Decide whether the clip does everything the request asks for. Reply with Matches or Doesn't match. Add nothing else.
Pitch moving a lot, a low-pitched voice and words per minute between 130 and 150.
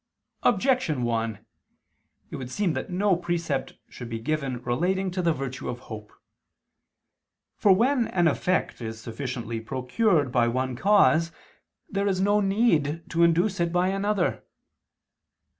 Doesn't match